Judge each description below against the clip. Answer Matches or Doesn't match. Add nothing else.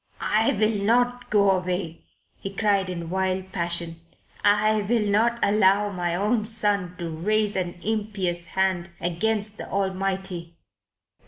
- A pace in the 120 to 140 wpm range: Matches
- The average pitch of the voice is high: Matches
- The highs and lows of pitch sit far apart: Doesn't match